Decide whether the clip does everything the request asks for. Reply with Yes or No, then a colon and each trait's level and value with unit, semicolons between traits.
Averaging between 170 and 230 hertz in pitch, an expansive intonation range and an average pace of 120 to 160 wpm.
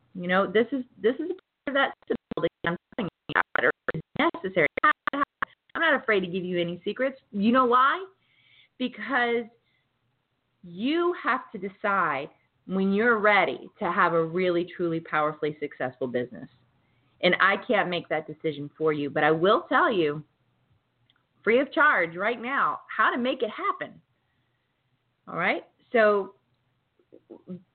Yes: medium, 185 Hz; wide, 8.7 semitones; average, 140 wpm